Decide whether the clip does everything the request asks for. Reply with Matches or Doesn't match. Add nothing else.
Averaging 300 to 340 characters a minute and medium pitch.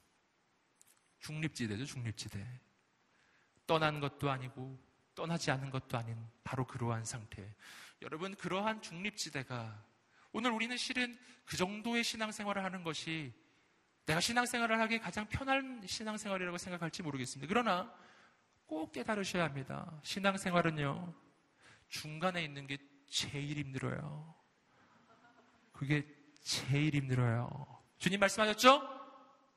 Doesn't match